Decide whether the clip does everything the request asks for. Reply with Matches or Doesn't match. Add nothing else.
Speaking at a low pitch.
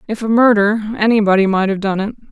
Doesn't match